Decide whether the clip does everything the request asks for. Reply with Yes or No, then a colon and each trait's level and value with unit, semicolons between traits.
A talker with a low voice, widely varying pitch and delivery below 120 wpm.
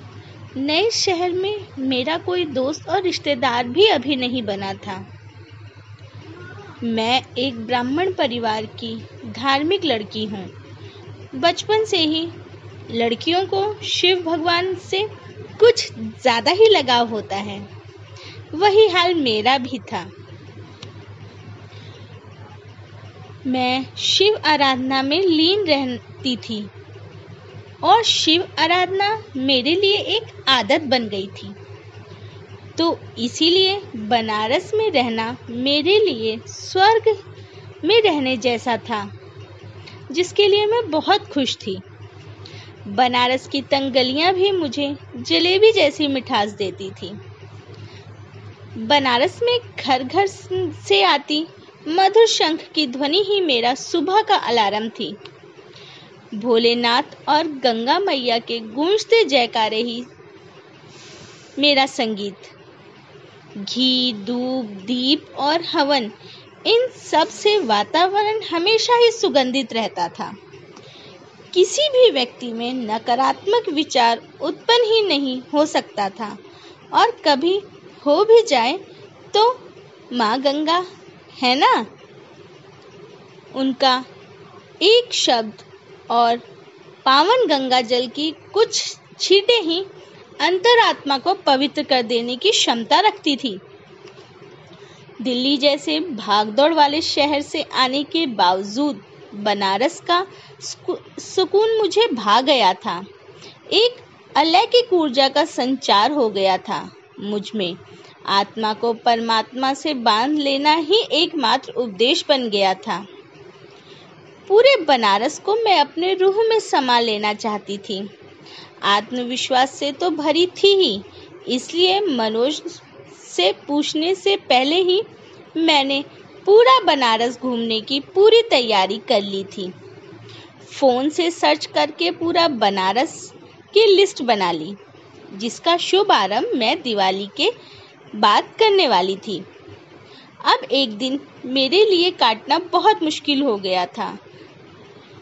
No: very high, 275 Hz; wide, 8.9 semitones; slow, 110 wpm